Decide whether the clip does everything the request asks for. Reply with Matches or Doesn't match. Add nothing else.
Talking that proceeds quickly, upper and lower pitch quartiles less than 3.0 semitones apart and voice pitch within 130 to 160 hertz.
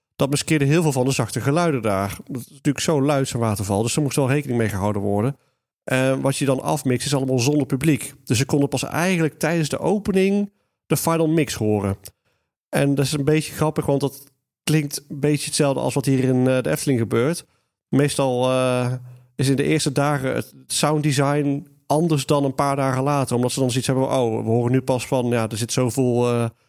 Matches